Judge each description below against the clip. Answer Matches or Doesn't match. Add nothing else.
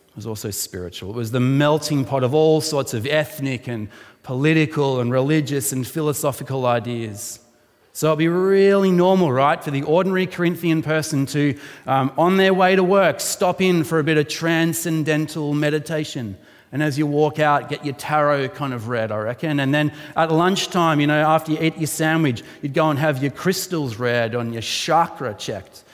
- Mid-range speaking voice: Matches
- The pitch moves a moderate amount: Matches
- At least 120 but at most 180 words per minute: Doesn't match